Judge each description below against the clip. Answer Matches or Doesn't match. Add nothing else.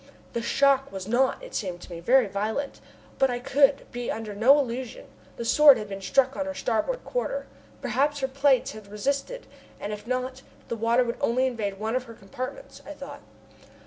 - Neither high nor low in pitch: Doesn't match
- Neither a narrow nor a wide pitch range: Matches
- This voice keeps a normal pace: Matches